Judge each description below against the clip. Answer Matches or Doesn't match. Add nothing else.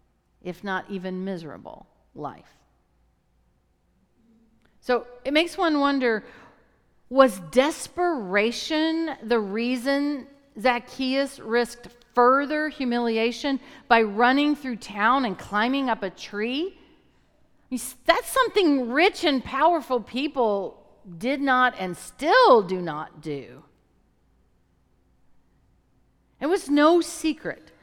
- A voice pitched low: Doesn't match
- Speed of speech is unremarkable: Doesn't match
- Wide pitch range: Matches